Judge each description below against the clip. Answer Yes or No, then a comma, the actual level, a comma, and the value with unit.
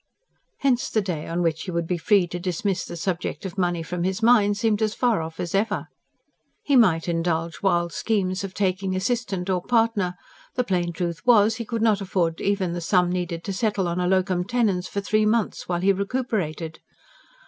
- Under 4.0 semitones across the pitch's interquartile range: Yes, average, 3.5 semitones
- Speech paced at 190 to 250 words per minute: Yes, average, 200 wpm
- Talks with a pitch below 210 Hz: Yes, medium, 185 Hz